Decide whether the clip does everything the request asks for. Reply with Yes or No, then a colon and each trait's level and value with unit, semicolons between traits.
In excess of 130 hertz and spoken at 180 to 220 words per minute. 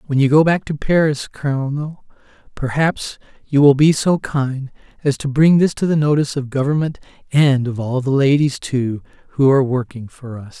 Yes: medium, 140 Hz; average, 185 wpm